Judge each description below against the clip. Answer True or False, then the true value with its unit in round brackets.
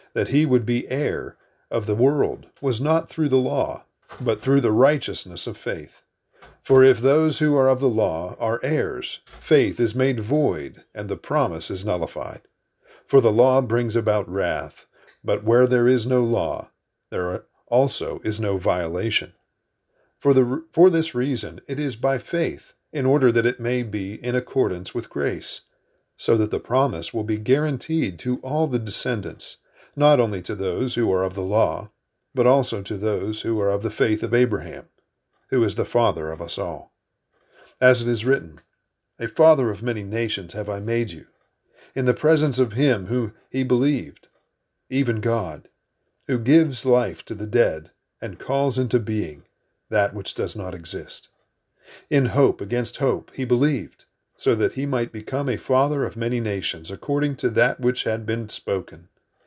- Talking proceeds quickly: False (175 wpm)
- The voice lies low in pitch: True (125 Hz)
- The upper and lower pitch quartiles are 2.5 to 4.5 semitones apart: True (3.8 semitones)